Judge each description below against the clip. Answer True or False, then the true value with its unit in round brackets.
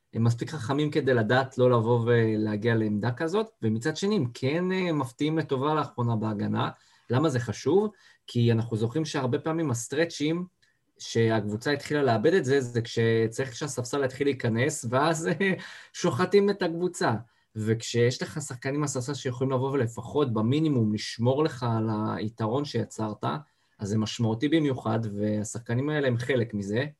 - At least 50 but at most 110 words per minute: False (140 wpm)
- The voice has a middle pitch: False (130 Hz)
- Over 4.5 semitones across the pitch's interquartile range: True (4.9 semitones)